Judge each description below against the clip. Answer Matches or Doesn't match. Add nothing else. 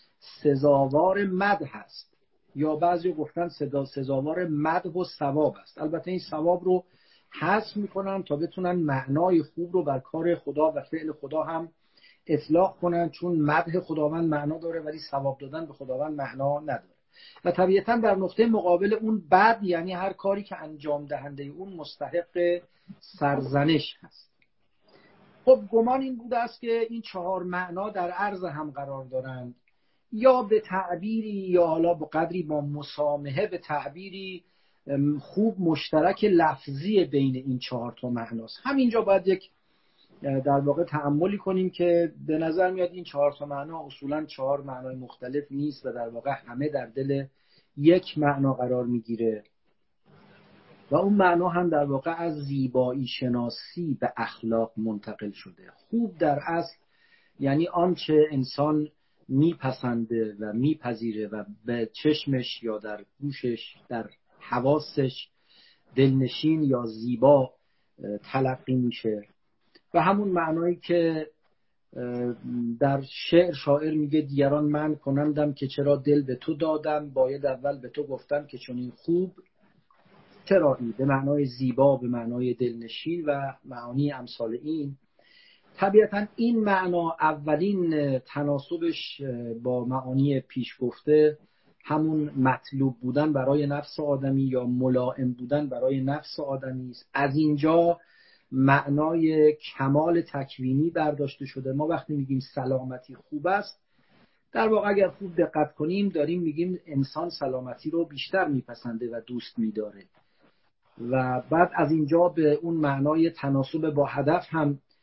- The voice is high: Doesn't match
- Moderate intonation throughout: Matches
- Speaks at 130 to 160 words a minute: Matches